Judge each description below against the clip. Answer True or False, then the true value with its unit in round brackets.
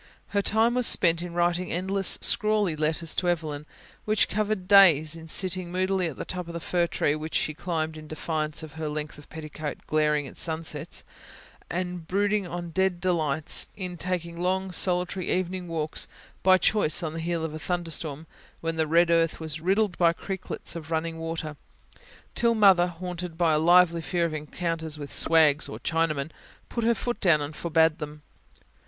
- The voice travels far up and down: False (2.6 semitones)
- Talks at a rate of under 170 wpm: False (180 wpm)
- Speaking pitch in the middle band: True (170 Hz)